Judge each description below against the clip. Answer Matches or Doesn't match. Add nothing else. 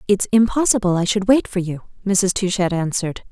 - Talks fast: Doesn't match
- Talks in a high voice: Matches